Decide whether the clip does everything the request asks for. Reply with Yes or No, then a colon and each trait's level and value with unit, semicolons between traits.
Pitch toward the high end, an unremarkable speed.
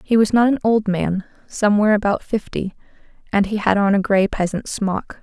Yes: high, 205 Hz; average, 195 wpm